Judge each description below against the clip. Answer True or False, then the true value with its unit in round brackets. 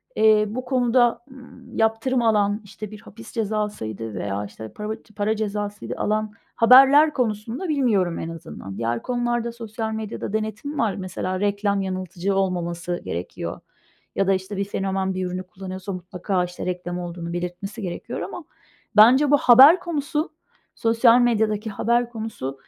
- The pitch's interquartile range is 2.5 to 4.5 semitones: True (4.1 semitones)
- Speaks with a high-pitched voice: True (210 Hz)